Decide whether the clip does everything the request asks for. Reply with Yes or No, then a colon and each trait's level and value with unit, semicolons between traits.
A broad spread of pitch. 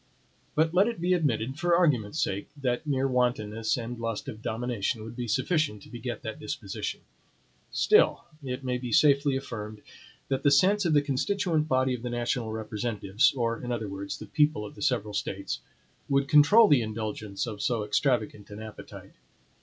No: average, 4.9 semitones